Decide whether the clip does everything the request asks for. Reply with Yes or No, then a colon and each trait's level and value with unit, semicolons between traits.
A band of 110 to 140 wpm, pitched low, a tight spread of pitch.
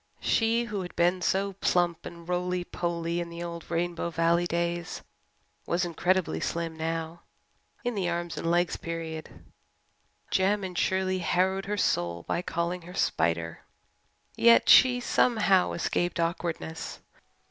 No: slow, 135 wpm; medium, 175 Hz; narrow, 1.9 semitones